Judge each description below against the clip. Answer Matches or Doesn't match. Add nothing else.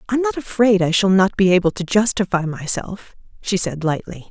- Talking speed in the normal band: Matches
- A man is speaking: Doesn't match